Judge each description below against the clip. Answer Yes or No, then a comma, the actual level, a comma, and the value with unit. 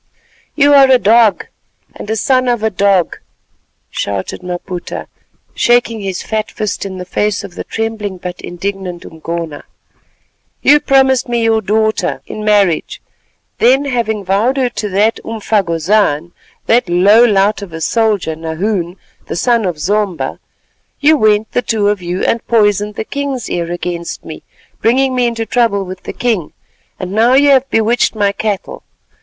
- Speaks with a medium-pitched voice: No, high, 210 Hz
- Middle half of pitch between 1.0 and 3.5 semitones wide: No, average, 4.3 semitones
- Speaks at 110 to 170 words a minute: Yes, average, 155 wpm